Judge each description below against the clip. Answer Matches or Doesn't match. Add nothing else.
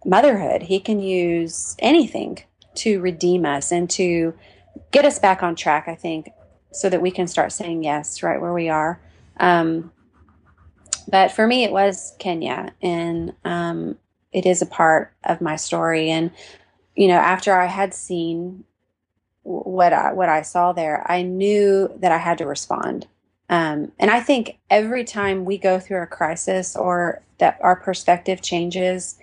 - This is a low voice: Doesn't match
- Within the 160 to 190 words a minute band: Matches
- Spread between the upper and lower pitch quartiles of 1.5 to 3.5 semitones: Matches